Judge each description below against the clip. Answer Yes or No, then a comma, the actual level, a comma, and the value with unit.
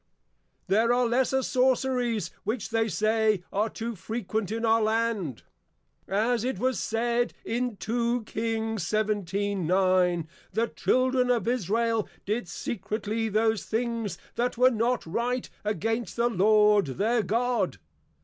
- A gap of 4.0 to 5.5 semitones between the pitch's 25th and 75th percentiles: No, narrow, 2.4 semitones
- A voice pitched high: Yes, high, 225 Hz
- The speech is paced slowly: Yes, slow, 125 wpm